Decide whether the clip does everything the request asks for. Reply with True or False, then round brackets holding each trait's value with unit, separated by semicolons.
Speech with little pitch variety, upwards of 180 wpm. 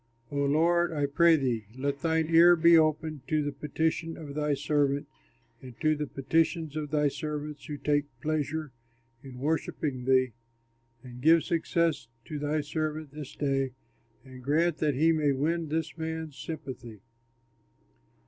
False (2.3 semitones; 150 wpm)